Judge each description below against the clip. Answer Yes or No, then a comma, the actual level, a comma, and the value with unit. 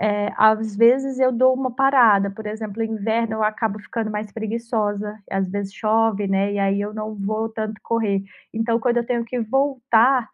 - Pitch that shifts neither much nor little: No, narrow, 2.1 semitones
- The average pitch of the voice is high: Yes, high, 220 Hz